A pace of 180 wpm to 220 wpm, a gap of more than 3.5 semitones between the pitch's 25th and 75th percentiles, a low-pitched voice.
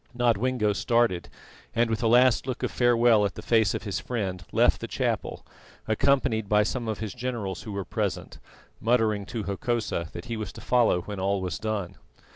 No: average, 190 wpm; average, 3.2 semitones; low, 110 Hz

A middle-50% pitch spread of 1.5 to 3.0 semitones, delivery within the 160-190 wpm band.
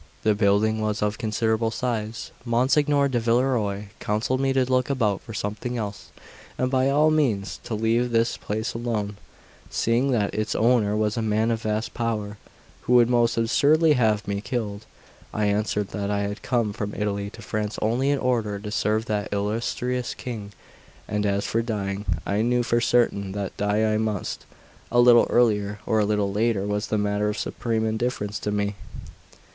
Yes: narrow, 2.6 semitones; average, 180 wpm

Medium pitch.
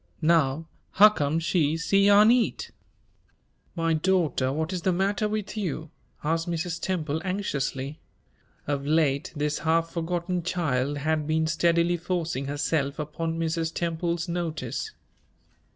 Yes: medium, 165 Hz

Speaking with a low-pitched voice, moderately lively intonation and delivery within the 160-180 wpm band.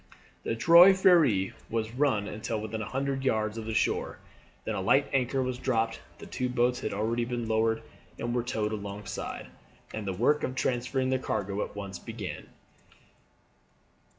Yes: low, 115 Hz; average, 3.1 semitones; average, 175 wpm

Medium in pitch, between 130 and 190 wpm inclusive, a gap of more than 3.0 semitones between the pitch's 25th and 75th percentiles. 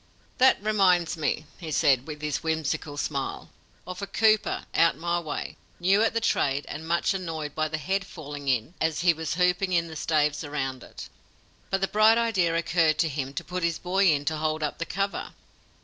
No: medium, 165 Hz; average, 200 wpm; average, 3.5 semitones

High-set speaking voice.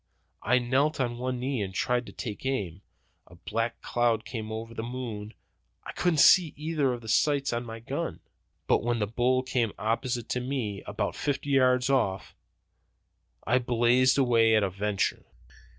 No: low, 120 Hz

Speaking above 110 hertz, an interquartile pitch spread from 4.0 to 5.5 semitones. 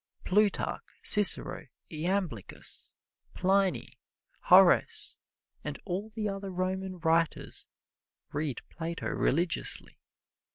No: medium, 185 Hz; average, 3.1 semitones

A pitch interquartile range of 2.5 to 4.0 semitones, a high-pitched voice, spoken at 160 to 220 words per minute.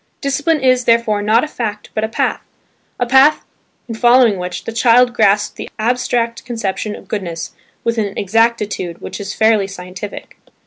Yes: average, 2.9 semitones; high, 225 Hz; average, 165 wpm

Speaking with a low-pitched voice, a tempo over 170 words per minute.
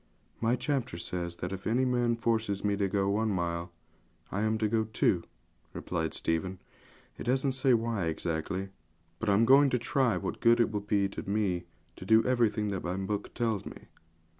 Yes: low, 105 Hz; average, 190 wpm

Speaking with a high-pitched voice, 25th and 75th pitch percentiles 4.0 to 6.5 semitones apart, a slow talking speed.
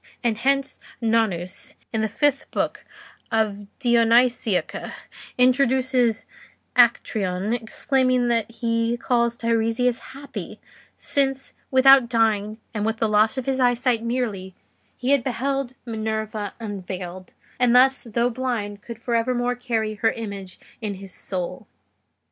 No: high, 230 Hz; average, 2.7 semitones; slow, 125 wpm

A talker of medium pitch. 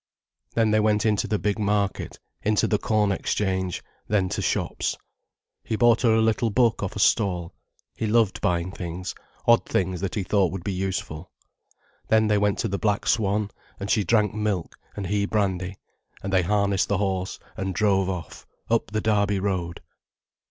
No: low, 100 Hz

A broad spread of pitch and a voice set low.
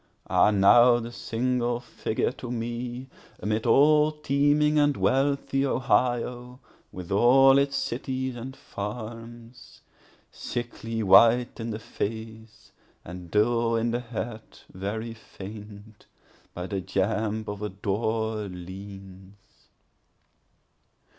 No: average, 3.0 semitones; low, 115 Hz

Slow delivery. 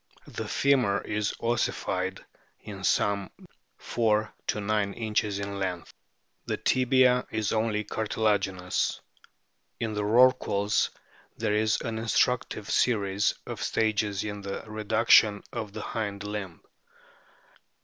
Yes: slow, 120 wpm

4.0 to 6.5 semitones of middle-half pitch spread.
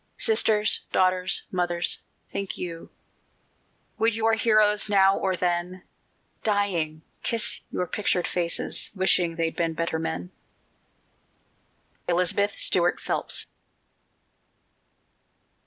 No: average, 3.3 semitones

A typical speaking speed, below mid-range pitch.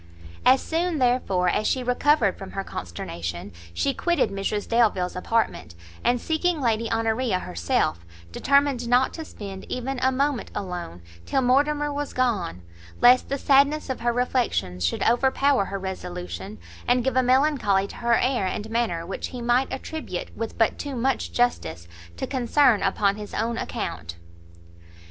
No: average, 155 wpm; high, 235 Hz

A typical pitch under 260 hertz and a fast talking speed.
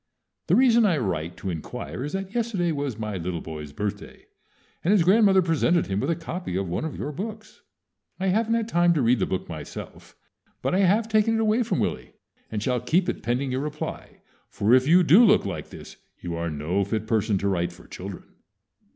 Yes: medium, 140 Hz; fast, 210 wpm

